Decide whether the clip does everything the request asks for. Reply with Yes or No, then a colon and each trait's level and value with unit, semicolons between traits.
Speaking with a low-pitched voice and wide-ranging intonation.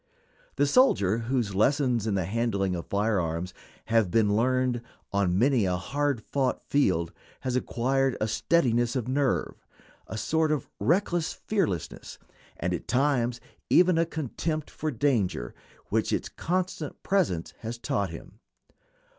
Yes: low, 120 Hz; wide, 6.2 semitones